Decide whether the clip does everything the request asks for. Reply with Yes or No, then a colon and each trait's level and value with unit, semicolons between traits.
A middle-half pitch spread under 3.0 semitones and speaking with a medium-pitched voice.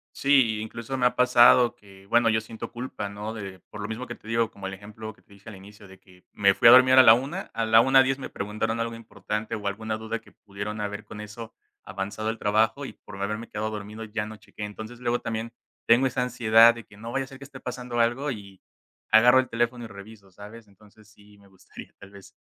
No: narrow, 2.6 semitones; low, 110 Hz